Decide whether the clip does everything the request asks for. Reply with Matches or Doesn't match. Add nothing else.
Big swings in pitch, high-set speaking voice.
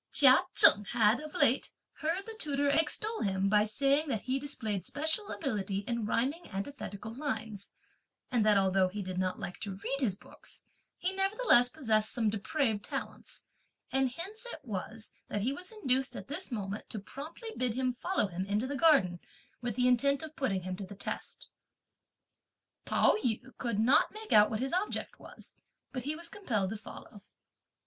Matches